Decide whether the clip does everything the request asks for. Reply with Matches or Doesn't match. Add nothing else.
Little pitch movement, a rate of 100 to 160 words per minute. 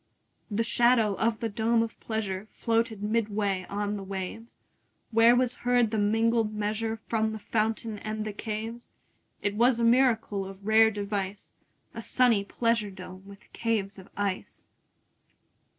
Matches